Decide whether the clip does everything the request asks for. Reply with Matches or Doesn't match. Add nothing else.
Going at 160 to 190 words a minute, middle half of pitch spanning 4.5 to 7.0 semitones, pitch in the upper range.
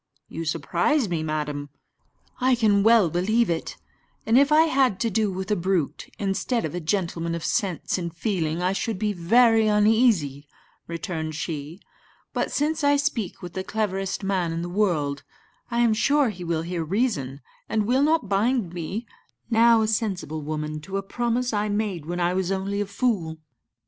Matches